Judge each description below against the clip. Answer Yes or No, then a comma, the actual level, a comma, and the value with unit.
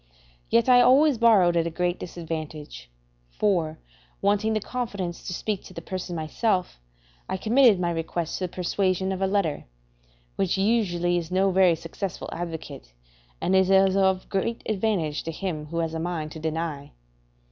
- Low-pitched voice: No, medium, 180 Hz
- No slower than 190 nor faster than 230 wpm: No, average, 165 wpm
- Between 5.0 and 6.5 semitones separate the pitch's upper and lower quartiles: No, average, 3.2 semitones